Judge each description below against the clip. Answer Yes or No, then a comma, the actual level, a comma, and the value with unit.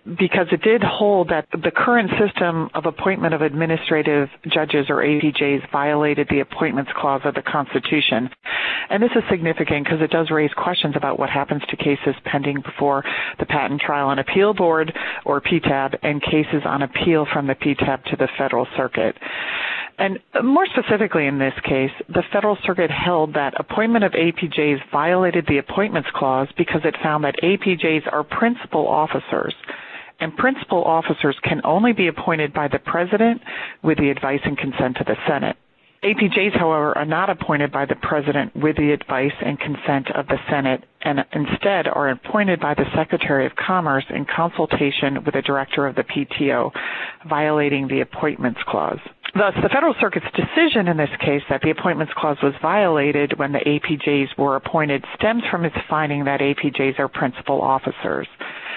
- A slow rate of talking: No, average, 170 wpm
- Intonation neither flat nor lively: Yes, average, 4.0 semitones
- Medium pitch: Yes, medium, 155 Hz